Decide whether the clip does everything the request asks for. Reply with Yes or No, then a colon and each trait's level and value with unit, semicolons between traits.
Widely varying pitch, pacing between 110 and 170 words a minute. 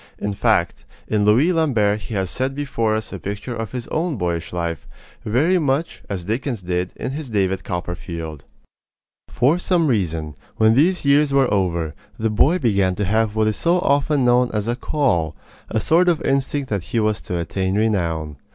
No: wide, 6.7 semitones; average, 190 wpm